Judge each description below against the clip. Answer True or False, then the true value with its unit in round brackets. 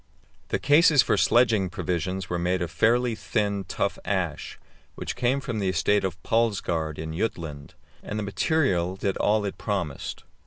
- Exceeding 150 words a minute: True (160 wpm)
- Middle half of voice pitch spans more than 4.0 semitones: True (4.5 semitones)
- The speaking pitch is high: False (100 Hz)